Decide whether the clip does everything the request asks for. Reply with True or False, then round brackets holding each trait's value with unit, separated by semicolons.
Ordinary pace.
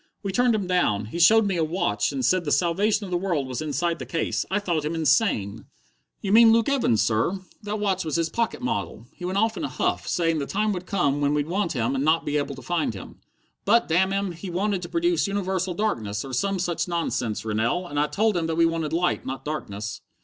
False (240 wpm)